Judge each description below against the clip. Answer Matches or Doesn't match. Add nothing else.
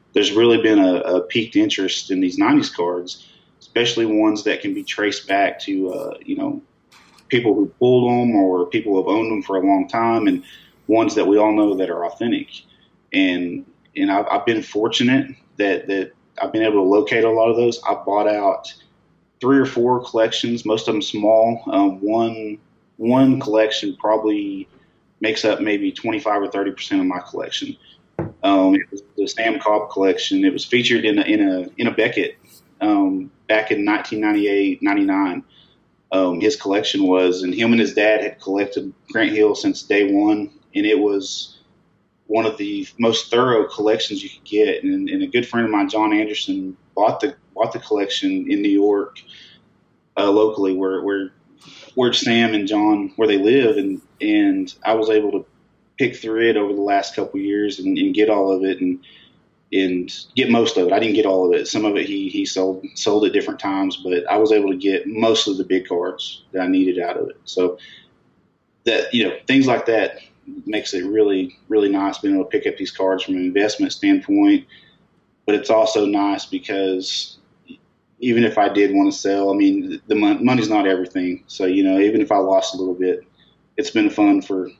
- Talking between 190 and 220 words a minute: Matches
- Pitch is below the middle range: Matches